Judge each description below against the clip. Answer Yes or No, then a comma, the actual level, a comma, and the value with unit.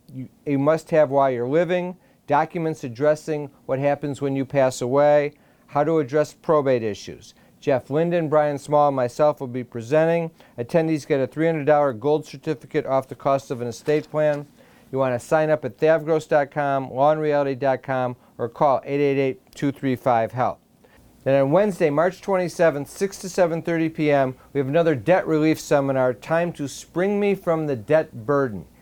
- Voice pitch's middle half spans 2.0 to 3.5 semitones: Yes, average, 2.8 semitones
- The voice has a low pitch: No, medium, 145 Hz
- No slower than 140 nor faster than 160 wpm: Yes, average, 155 wpm